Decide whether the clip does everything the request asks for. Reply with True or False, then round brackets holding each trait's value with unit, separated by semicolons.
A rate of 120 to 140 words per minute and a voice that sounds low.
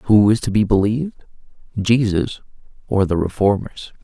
True (135 wpm; 105 Hz)